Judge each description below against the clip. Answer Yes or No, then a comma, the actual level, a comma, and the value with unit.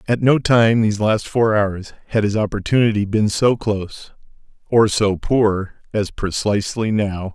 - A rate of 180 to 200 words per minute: No, average, 140 wpm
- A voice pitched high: No, low, 105 Hz